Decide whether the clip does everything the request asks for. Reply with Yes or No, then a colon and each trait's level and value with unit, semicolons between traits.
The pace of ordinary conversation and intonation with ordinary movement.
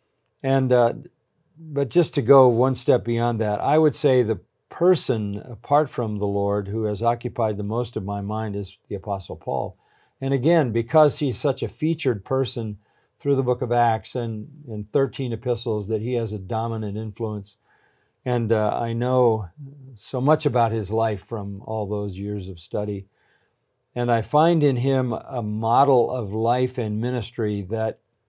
Yes: average, 170 wpm; average, 3.7 semitones